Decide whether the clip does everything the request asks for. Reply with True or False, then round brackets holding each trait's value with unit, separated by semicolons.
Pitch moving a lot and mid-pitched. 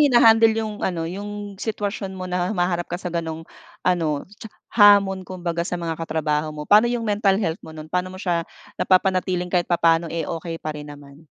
False (3.5 semitones; 180 Hz)